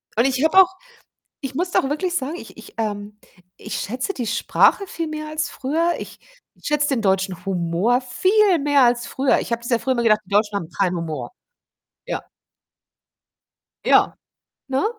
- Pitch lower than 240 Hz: No, very high, 255 Hz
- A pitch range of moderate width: No, wide, 6.6 semitones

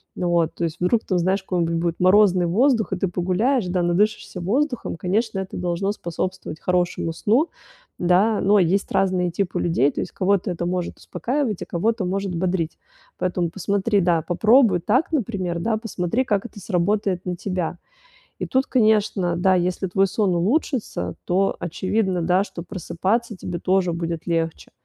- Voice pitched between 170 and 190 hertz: Yes, medium, 185 Hz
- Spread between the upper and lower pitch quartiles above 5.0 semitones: No, average, 3.2 semitones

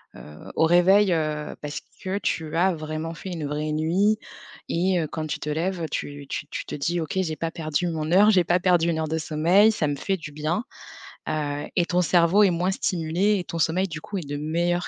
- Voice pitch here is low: No, medium, 165 Hz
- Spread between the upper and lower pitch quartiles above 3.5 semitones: No, average, 2.8 semitones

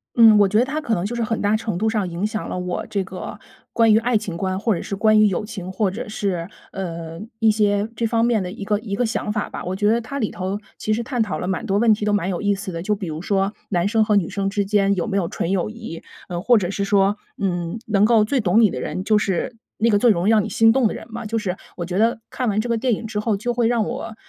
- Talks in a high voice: Yes, high, 210 Hz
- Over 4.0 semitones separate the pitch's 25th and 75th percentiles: No, average, 2.8 semitones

